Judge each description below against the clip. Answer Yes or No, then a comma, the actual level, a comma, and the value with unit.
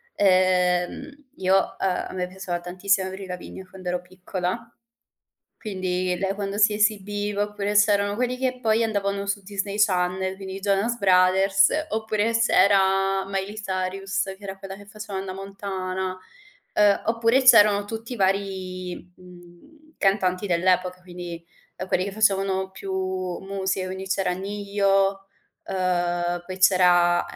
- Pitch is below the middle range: No, high, 195 Hz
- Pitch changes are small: Yes, narrow, 1.8 semitones